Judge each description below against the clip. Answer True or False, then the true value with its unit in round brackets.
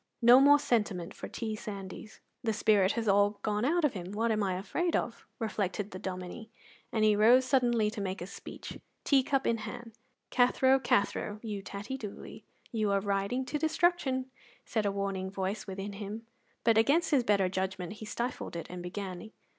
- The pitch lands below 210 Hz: False (215 Hz)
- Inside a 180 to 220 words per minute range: True (185 wpm)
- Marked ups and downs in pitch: False (3.7 semitones)